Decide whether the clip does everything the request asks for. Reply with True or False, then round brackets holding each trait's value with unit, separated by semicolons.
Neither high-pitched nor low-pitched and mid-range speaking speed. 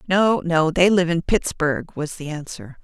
True (165 Hz; 190 wpm)